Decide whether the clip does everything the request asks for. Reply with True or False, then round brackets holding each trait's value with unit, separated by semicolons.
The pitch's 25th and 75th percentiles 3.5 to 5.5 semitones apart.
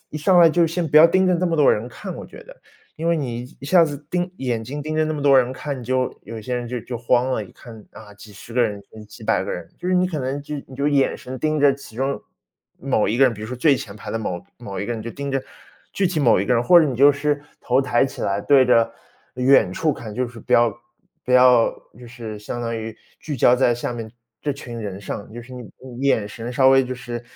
True (3.9 semitones)